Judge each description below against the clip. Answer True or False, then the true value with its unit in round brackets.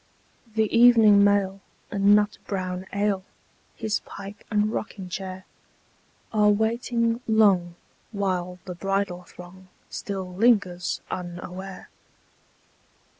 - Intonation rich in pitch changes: False (2.4 semitones)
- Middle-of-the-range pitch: False (200 Hz)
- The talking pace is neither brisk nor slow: False (100 wpm)